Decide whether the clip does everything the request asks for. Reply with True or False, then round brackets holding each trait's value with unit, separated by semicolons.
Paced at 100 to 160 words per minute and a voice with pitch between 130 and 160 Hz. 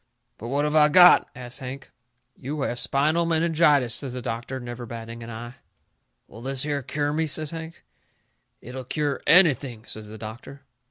False (170 wpm; 135 Hz)